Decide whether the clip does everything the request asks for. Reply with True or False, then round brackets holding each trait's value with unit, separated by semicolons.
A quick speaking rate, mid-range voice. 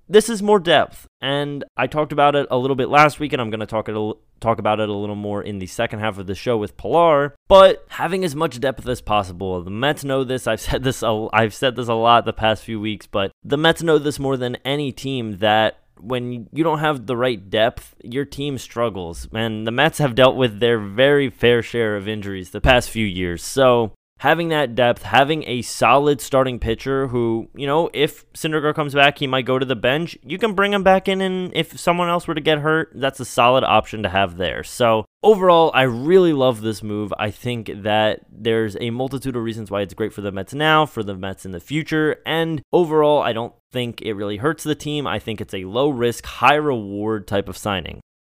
False (235 wpm; 125 Hz)